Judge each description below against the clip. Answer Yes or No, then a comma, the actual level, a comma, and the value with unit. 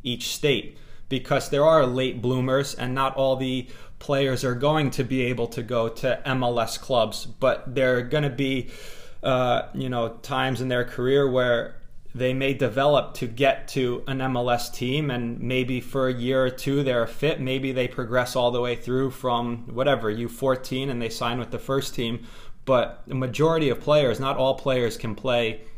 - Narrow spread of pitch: Yes, narrow, 1.9 semitones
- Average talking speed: Yes, average, 190 wpm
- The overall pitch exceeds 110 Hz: Yes, low, 130 Hz